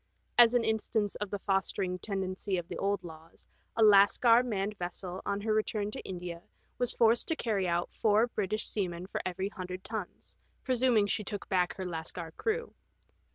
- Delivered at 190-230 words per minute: No, average, 175 wpm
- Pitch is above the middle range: Yes, high, 200 Hz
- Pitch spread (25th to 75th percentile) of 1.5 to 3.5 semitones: Yes, average, 3.2 semitones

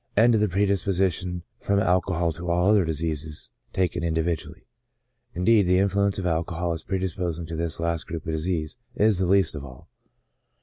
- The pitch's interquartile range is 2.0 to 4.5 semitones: Yes, average, 2.8 semitones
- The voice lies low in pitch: Yes, very low, 90 Hz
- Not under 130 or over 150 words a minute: No, average, 170 wpm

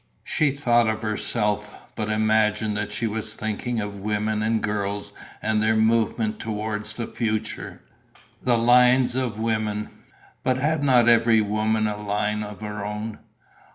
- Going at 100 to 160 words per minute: Yes, average, 155 wpm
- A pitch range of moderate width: No, narrow, 1.6 semitones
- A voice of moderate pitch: No, low, 110 Hz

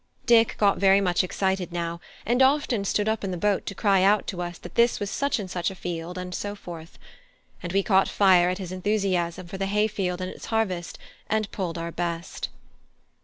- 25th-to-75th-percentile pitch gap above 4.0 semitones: No, average, 2.7 semitones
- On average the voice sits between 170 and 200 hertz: Yes, high, 190 Hz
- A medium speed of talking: No, fast, 215 wpm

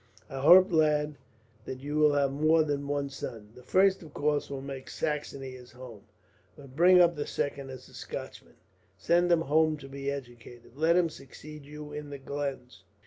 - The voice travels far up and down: No, narrow, 2.4 semitones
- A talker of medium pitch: Yes, medium, 145 Hz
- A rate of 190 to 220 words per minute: Yes, average, 195 wpm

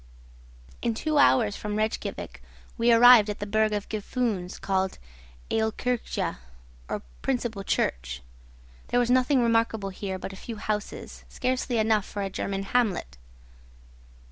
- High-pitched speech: Yes, high, 220 Hz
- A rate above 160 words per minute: No, slow, 135 wpm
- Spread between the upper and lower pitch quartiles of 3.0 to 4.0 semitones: Yes, average, 3.3 semitones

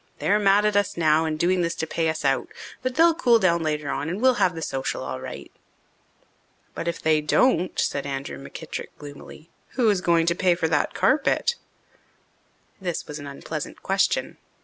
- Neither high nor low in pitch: Yes, medium, 170 Hz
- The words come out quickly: No, average, 190 wpm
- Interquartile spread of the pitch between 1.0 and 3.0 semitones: No, average, 4.7 semitones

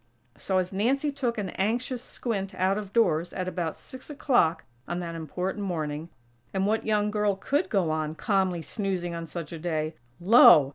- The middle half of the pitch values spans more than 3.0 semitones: Yes, average, 4.2 semitones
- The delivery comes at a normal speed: Yes, average, 180 wpm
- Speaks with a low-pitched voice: No, high, 190 Hz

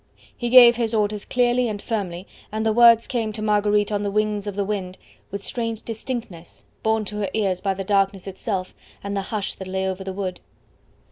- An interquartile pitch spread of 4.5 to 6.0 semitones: No, narrow, 2.4 semitones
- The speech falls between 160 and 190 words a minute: No, fast, 205 wpm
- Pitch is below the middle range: No, high, 210 Hz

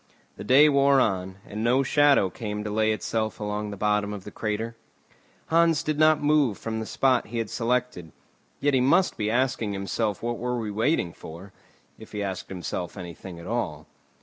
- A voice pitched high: No, low, 110 Hz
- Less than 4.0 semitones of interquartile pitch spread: No, average, 4.3 semitones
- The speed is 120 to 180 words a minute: No, average, 190 wpm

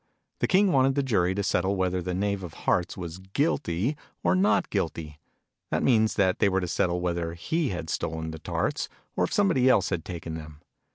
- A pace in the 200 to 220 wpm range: Yes, fast, 205 wpm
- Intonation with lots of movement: No, average, 4.9 semitones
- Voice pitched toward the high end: No, very low, 95 Hz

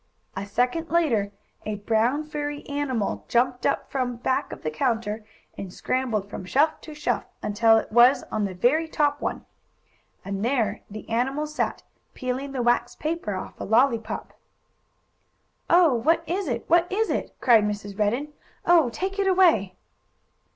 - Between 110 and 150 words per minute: No, average, 160 wpm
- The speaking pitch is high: Yes, very high, 250 Hz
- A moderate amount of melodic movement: No, wide, 5.8 semitones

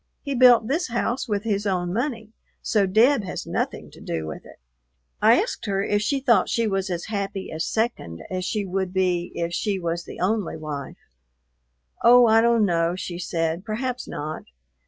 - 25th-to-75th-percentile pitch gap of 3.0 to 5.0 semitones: Yes, average, 4.7 semitones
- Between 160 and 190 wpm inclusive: Yes, average, 185 wpm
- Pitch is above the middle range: Yes, high, 200 Hz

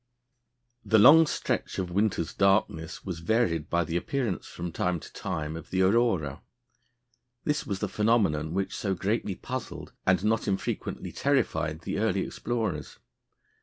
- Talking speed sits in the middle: Yes, average, 145 wpm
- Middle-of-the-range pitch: No, very low, 95 Hz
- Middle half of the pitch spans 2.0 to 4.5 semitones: No, average, 4.9 semitones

